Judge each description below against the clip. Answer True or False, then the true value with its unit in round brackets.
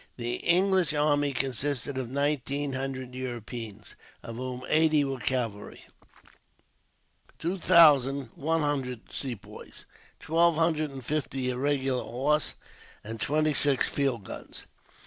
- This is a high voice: False (135 Hz)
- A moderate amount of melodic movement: True (3.2 semitones)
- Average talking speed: False (115 wpm)